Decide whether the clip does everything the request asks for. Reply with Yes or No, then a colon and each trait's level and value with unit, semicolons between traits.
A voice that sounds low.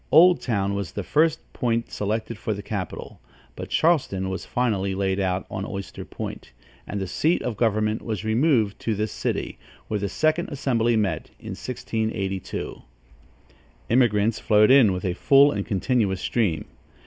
Yes: low, 110 Hz